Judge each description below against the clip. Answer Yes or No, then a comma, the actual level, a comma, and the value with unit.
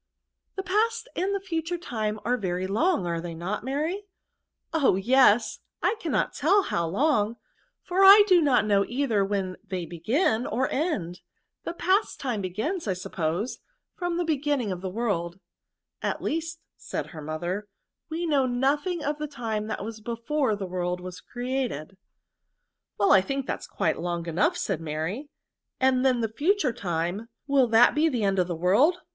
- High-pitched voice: Yes, high, 235 Hz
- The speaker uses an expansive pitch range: Yes, wide, 8.4 semitones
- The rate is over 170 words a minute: Yes, average, 180 wpm